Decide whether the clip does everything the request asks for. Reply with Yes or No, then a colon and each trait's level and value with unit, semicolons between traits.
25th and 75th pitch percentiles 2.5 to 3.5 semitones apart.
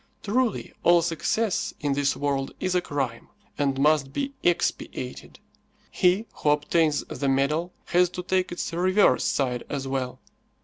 No: average, 4.6 semitones